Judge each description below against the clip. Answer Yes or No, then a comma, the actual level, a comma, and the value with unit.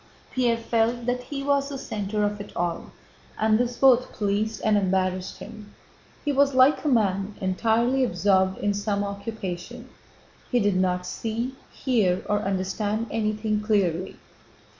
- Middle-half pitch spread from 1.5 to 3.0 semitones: No, average, 3.6 semitones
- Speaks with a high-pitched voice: Yes, high, 215 Hz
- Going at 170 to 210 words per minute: No, average, 145 wpm